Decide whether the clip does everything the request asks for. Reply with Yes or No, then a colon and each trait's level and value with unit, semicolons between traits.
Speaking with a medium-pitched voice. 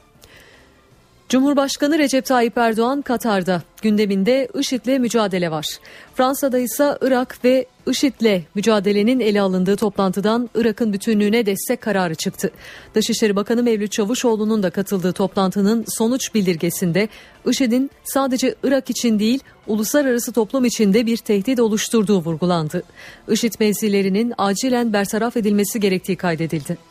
No: high, 220 Hz